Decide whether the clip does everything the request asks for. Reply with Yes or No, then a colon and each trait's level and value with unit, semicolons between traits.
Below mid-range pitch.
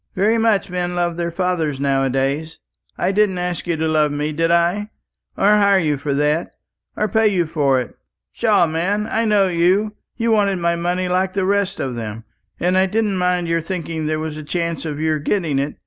No: medium, 175 Hz